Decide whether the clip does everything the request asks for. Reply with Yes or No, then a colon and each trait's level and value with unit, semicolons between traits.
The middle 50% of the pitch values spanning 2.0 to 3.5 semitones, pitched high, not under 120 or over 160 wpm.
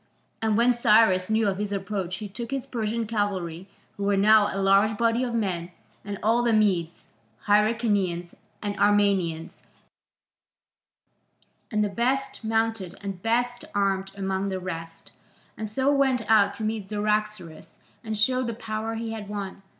Yes: narrow, 2.6 semitones; high, 210 Hz; average, 155 wpm